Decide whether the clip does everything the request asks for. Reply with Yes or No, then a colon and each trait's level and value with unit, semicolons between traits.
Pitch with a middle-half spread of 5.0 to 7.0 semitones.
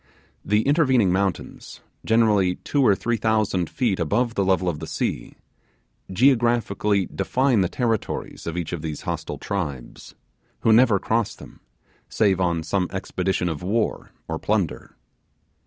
No: average, 4.2 semitones